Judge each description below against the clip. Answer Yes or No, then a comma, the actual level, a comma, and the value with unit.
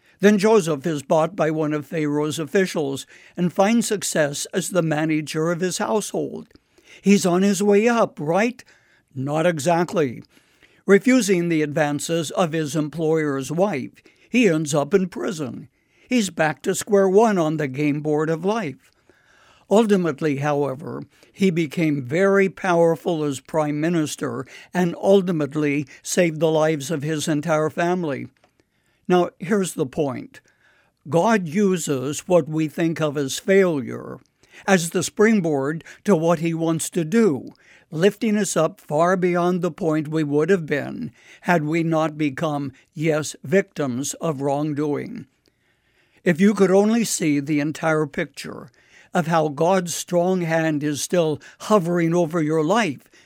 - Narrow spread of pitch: No, average, 3.8 semitones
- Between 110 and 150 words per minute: Yes, average, 140 wpm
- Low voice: No, medium, 165 Hz